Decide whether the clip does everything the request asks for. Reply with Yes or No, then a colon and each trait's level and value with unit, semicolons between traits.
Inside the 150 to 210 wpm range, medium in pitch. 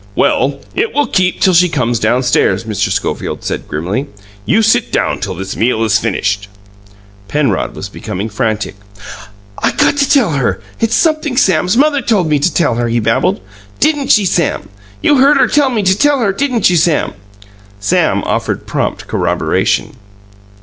Yes: average, 170 wpm; medium, 170 Hz